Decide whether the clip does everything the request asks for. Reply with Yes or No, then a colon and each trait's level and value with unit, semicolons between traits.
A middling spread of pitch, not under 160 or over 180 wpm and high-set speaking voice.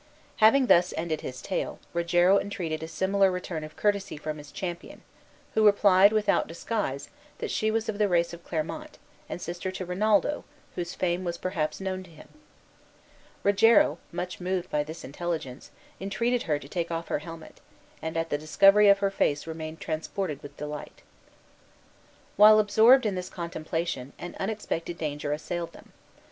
No: average, 4.0 semitones; average, 165 wpm; medium, 175 Hz